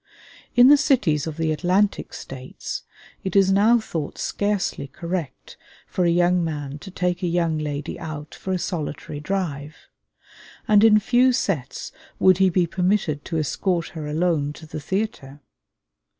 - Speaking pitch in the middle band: Yes, medium, 175 Hz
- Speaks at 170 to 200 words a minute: No, average, 155 wpm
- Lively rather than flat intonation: No, average, 4.3 semitones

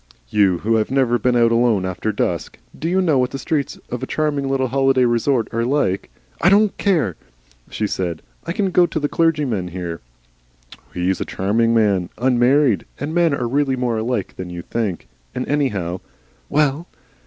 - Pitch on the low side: Yes, low, 125 Hz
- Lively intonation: Yes, wide, 5.9 semitones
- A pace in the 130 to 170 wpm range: No, average, 190 wpm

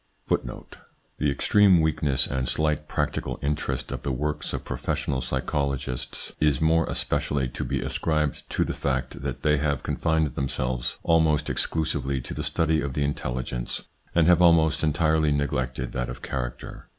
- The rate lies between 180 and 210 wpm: No, average, 160 wpm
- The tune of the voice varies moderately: Yes, average, 3.3 semitones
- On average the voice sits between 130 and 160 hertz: No, very low, 70 Hz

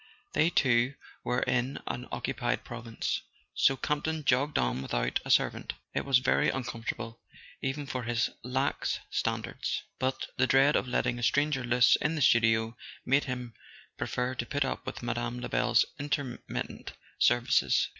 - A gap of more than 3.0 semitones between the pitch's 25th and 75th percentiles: No, narrow, 2.4 semitones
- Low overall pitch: Yes, low, 125 Hz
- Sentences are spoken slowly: No, average, 150 wpm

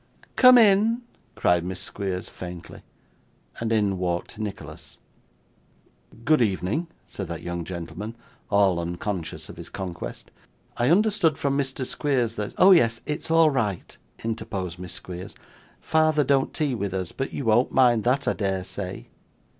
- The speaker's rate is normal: Yes, average, 150 wpm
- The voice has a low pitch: Yes, low, 110 Hz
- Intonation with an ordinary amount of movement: No, wide, 7.3 semitones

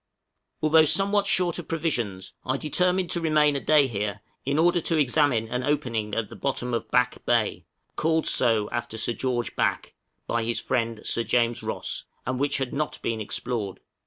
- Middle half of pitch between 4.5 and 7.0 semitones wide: Yes, average, 5.1 semitones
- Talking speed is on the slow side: No, average, 180 wpm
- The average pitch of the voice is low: Yes, low, 125 Hz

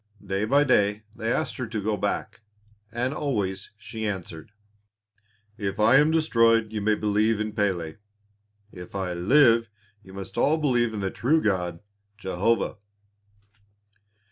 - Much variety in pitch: No, average, 3.2 semitones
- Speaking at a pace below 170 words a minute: Yes, average, 140 wpm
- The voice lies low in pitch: Yes, low, 110 Hz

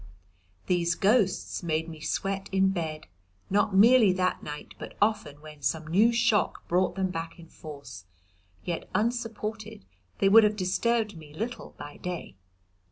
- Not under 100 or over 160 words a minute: Yes, average, 155 wpm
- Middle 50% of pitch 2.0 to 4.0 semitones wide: No, average, 4.9 semitones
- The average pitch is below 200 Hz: Yes, medium, 185 Hz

